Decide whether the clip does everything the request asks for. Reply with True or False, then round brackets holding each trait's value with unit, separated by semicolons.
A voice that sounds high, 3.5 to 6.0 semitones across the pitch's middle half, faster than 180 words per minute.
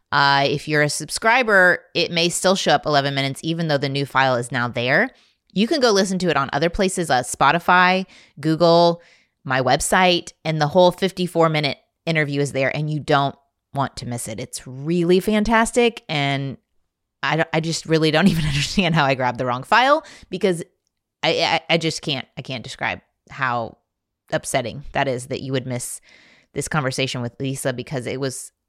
False (150 Hz; 4.6 semitones; 190 wpm)